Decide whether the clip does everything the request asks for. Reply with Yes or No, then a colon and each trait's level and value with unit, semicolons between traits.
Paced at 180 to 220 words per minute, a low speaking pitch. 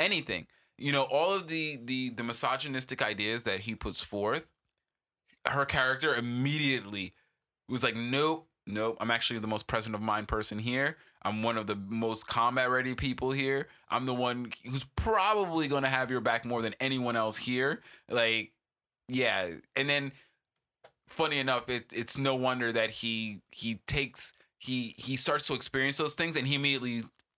No: average, 170 wpm; low, 125 Hz